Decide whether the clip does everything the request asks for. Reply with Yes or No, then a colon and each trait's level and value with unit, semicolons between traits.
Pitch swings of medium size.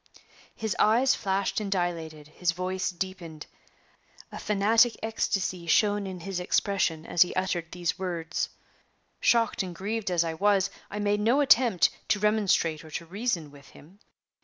Yes: average, 3.5 semitones